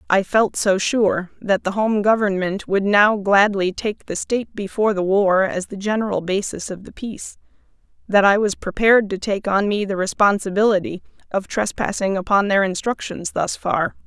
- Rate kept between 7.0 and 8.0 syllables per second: No, 4.8 syllables/s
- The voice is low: No, high, 200 Hz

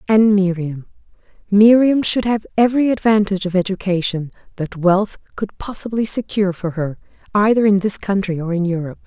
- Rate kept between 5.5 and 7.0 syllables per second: Yes, 5.6 syllables/s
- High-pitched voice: Yes, high, 195 Hz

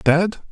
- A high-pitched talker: No, medium, 175 Hz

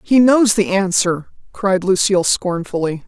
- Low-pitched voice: No, high, 190 Hz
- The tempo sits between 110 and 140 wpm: Yes, slow, 135 wpm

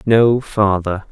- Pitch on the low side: Yes, low, 105 Hz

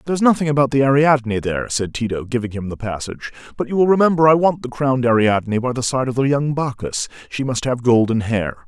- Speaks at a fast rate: Yes, fast, 230 wpm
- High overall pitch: No, low, 130 Hz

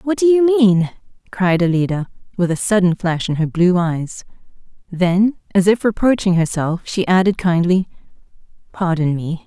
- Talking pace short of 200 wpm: Yes, average, 150 wpm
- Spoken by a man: No, female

